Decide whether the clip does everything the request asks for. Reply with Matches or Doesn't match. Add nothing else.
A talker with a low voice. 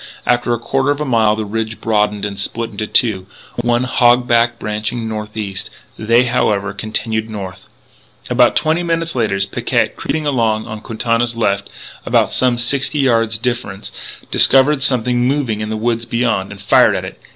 Matches